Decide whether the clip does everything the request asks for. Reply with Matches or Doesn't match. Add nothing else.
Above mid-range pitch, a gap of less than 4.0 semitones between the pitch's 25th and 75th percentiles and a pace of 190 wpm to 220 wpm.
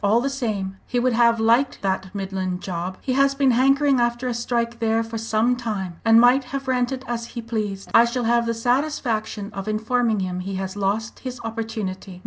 Matches